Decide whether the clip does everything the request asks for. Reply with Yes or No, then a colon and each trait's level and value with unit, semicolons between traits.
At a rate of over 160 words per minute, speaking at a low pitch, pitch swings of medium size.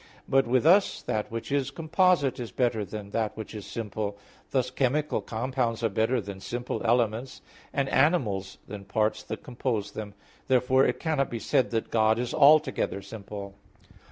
Yes: average, 170 wpm; low, 120 Hz; average, 3.9 semitones